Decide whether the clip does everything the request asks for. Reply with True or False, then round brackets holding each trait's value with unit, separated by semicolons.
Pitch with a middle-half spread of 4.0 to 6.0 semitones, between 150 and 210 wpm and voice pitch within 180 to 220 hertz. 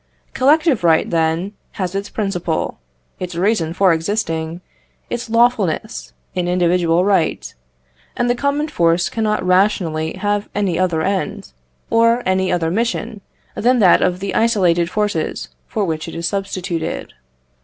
False (4.3 semitones; 135 wpm; 185 Hz)